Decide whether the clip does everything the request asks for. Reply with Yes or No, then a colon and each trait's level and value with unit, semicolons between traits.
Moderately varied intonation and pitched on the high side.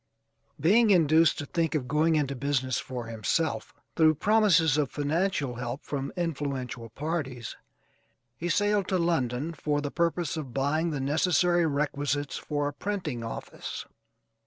No: average, 3.7 semitones; medium, 150 Hz